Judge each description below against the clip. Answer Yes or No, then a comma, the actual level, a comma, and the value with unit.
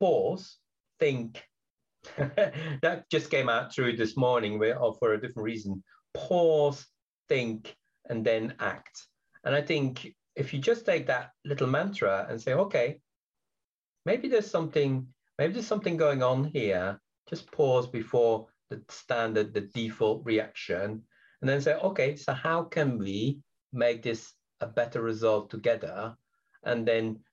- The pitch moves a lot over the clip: No, average, 4.9 semitones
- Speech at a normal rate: Yes, average, 145 wpm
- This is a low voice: Yes, low, 125 Hz